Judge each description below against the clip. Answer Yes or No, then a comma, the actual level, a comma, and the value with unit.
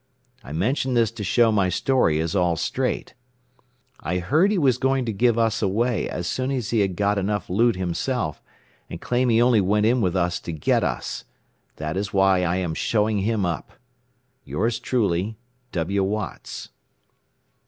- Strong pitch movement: No, average, 4.7 semitones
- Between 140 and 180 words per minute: Yes, average, 175 wpm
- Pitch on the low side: Yes, low, 105 Hz